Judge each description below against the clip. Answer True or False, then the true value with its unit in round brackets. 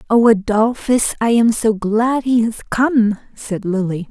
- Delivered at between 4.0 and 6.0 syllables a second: False (3.6 syllables/s)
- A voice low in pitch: False (220 Hz)